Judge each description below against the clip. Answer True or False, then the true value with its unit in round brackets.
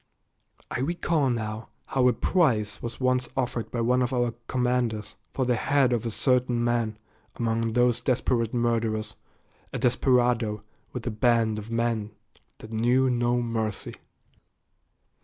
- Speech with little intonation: True (1.9 semitones)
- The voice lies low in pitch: True (120 Hz)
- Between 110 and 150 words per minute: True (140 wpm)